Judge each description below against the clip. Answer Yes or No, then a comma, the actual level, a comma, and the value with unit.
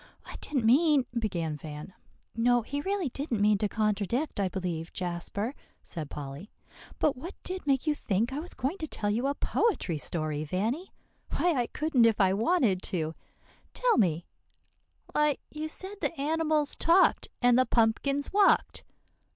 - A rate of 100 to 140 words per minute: No, average, 160 wpm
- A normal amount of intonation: No, wide, 7.9 semitones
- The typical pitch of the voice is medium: No, high, 240 Hz